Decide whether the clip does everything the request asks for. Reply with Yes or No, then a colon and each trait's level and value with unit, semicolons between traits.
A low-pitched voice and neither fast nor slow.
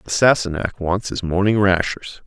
Yes: very low, 95 Hz; average, 160 wpm